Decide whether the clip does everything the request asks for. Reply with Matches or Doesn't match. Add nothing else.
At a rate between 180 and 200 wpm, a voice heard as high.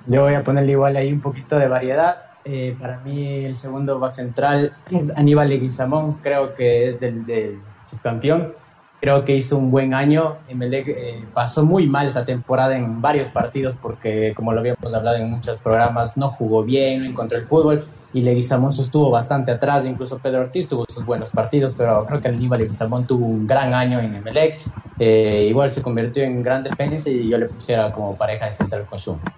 Doesn't match